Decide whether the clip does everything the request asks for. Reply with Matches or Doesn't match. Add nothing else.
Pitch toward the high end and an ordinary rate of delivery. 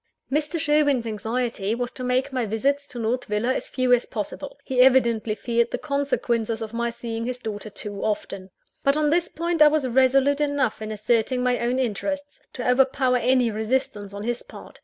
Matches